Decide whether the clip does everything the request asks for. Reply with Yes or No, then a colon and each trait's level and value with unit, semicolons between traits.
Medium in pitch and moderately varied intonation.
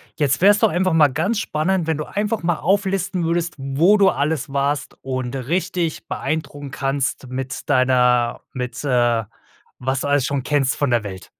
Yes: medium, 145 Hz; average, 4.9 semitones